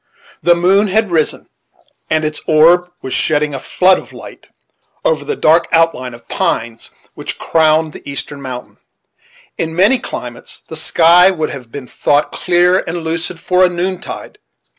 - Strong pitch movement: No, average, 3.3 semitones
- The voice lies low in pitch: No, medium, 165 Hz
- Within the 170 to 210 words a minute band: No, average, 160 wpm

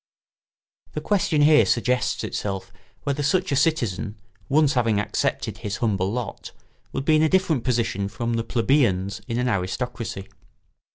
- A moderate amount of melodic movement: No, wide, 6.1 semitones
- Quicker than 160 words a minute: No, average, 155 wpm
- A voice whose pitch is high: No, low, 120 Hz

